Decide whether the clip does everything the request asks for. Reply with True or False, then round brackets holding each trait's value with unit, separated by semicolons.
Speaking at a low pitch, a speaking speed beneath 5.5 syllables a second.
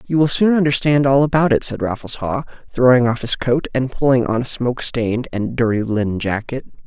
False (125 Hz; 5.6 syllables/s)